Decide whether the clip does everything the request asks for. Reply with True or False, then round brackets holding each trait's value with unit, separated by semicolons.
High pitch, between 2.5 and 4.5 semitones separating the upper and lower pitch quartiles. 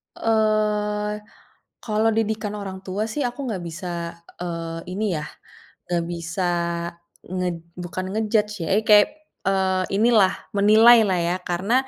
True (210 Hz; 2.8 semitones)